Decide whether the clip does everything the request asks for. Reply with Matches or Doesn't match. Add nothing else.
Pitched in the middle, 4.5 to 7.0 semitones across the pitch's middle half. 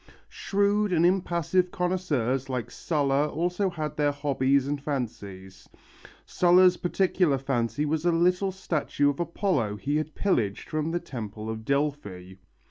Matches